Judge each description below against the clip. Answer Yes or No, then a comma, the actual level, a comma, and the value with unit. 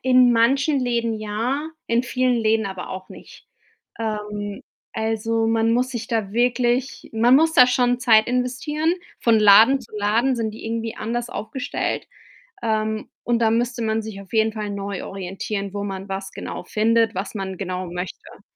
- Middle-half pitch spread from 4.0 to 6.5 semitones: No, average, 2.8 semitones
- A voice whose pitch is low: No, high, 225 Hz